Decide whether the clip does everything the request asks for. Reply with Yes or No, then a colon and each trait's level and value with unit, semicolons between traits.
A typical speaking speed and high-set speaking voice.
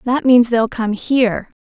Yes: average, 185 wpm; high, 235 Hz